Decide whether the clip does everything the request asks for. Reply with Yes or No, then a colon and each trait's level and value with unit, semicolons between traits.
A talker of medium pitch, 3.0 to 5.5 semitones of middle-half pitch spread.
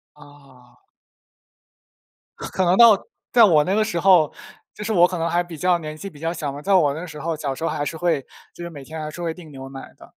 Yes: medium, 165 Hz; average, 3.5 semitones